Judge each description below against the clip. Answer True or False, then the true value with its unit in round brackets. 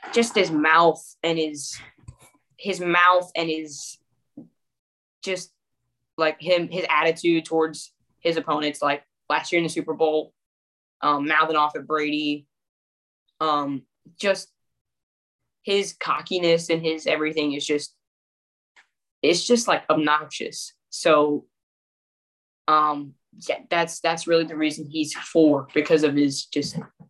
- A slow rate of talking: True (125 wpm)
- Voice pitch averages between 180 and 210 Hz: False (155 Hz)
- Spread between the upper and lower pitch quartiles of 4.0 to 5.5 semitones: False (2.7 semitones)